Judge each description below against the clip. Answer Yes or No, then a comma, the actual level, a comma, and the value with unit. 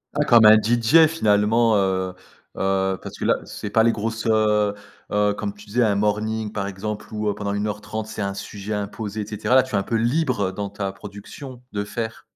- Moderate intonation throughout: No, narrow, 1.7 semitones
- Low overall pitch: Yes, low, 105 Hz